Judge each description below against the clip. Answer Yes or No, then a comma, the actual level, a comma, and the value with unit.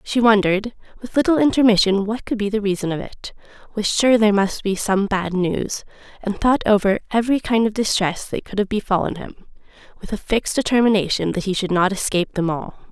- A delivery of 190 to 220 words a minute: Yes, average, 200 wpm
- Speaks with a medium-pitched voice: No, high, 210 Hz